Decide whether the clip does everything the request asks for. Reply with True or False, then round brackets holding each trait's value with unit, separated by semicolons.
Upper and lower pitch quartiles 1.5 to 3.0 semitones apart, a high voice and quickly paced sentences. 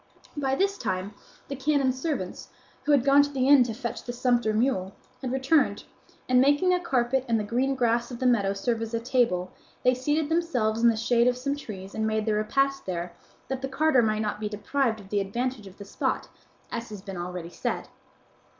False (4.0 semitones; 240 Hz; 215 wpm)